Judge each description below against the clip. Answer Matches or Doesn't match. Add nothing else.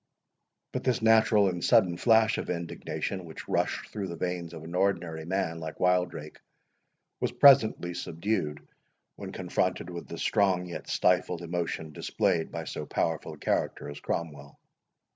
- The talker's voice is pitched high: Doesn't match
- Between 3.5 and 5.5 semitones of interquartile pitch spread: Doesn't match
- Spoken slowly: Doesn't match